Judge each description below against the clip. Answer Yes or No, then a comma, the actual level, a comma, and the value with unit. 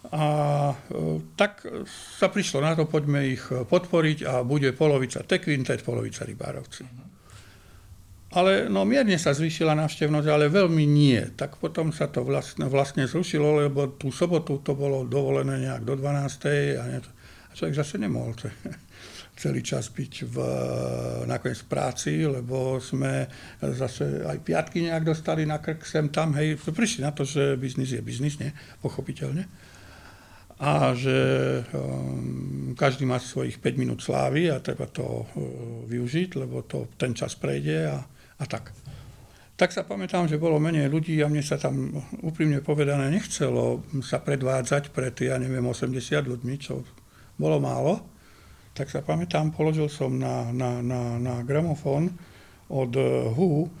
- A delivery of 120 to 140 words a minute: No, average, 150 wpm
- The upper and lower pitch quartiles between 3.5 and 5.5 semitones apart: Yes, average, 4.0 semitones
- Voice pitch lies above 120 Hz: Yes, low, 135 Hz